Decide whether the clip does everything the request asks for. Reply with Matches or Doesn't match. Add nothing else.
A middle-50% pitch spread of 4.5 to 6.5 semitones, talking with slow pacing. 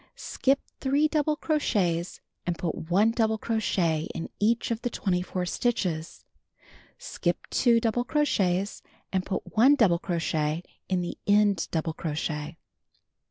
Matches